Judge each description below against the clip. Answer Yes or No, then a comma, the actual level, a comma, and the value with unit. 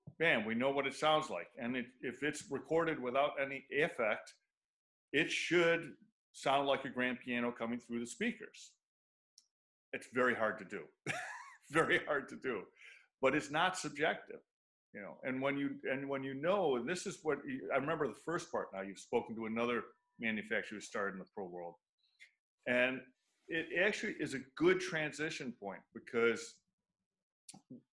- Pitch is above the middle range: No, low, 135 Hz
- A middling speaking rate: Yes, average, 170 wpm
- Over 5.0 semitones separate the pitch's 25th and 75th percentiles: No, average, 4.4 semitones